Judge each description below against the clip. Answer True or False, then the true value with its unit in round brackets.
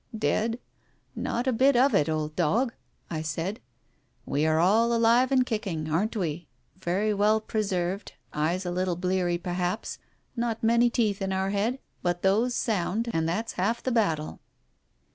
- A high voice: True (200 Hz)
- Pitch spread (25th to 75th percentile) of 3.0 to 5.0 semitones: True (4.7 semitones)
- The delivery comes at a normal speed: True (170 wpm)